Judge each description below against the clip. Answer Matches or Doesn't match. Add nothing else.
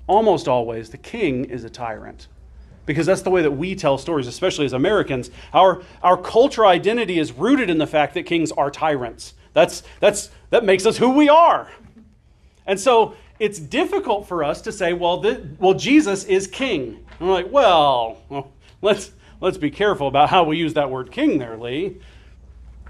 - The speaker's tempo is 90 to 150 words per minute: Doesn't match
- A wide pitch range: Matches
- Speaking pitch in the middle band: Matches